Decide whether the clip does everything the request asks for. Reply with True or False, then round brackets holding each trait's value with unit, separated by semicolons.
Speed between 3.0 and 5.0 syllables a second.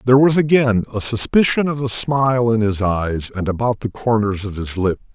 False (5.3 syllables/s)